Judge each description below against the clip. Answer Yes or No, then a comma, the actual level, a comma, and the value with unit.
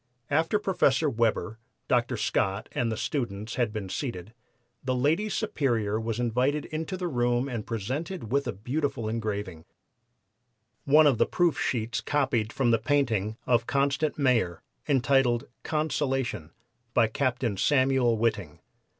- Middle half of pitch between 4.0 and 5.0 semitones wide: Yes, average, 4.4 semitones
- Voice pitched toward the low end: Yes, low, 125 Hz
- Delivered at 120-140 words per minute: Yes, slow, 135 wpm